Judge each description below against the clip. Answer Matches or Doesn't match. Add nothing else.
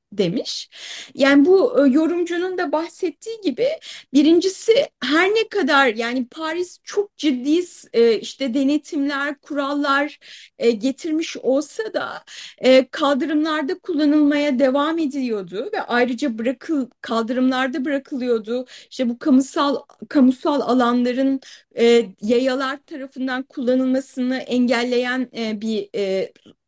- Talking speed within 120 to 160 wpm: Doesn't match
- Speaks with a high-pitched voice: Matches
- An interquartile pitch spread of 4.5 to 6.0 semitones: Doesn't match